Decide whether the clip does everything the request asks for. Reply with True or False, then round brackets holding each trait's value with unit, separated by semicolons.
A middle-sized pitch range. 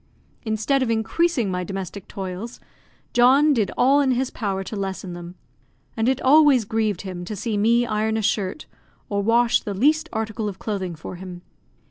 True (4.1 semitones)